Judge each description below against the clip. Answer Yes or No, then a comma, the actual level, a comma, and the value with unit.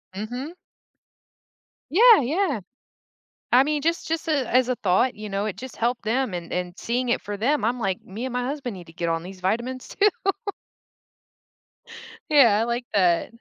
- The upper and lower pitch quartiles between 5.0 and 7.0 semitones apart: Yes, average, 5.3 semitones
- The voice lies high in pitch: Yes, high, 240 Hz